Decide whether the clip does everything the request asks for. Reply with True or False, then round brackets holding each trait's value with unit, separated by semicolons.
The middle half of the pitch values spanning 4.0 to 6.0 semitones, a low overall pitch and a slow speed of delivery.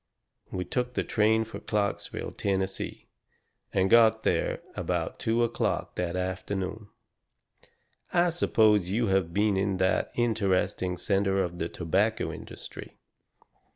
False (3.1 semitones; 100 Hz; 120 wpm)